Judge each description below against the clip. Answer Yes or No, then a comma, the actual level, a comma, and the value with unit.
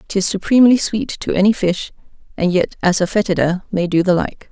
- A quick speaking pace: No, average, 185 wpm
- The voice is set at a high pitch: Yes, high, 195 Hz